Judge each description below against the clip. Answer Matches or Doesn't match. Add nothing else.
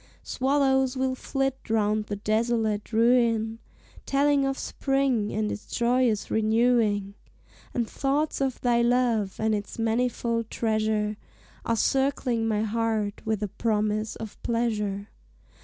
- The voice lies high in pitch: Matches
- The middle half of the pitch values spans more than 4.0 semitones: Doesn't match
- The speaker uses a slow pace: Matches